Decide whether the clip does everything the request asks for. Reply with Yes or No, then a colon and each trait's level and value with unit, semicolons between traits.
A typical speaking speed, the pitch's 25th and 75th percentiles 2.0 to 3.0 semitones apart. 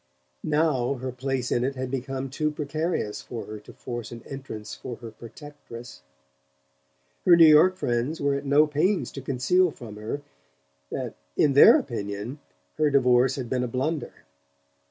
No: average, 160 wpm; average, 3.4 semitones